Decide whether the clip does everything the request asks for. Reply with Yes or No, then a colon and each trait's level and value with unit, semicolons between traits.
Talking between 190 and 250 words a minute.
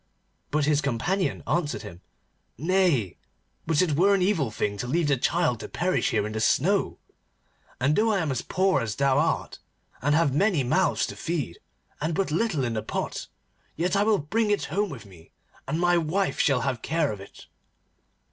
Yes: average, 195 wpm